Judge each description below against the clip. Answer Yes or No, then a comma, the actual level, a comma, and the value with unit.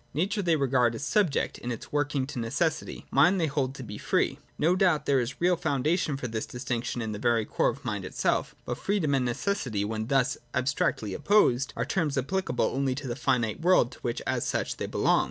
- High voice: No, low, 135 Hz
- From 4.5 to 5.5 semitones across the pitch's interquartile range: Yes, average, 5.0 semitones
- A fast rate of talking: Yes, fast, 220 wpm